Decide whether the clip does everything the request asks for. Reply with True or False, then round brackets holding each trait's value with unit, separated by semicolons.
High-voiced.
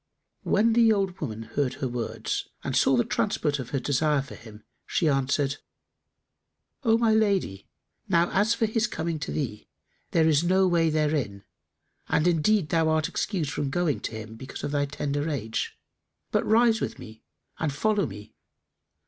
False (155 Hz)